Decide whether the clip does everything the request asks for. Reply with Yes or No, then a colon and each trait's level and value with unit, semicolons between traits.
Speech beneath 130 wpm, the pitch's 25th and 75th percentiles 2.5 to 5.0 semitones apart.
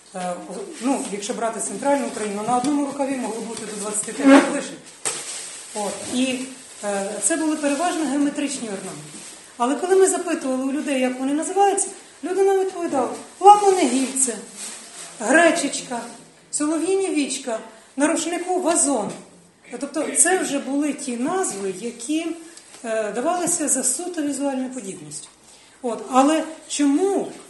No: average, 110 wpm; wide, 5.6 semitones